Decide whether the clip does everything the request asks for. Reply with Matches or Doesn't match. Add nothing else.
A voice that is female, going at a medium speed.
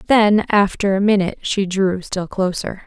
Matches